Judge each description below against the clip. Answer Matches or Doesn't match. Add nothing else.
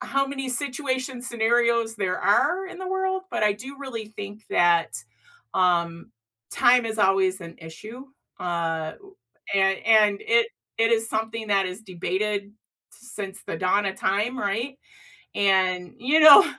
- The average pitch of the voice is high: Matches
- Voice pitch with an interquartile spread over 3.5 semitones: Matches